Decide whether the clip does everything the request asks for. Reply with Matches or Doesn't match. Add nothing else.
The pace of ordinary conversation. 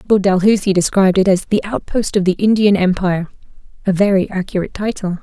Matches